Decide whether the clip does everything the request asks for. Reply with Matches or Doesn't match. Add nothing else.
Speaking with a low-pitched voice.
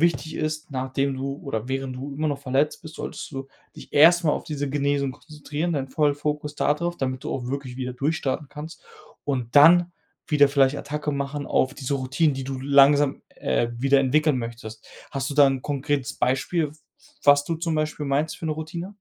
Doesn't match